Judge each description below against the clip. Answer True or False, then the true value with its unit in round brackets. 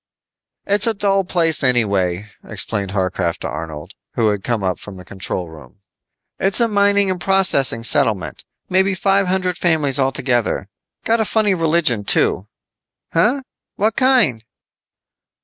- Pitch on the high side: False (145 Hz)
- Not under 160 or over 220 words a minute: False (140 wpm)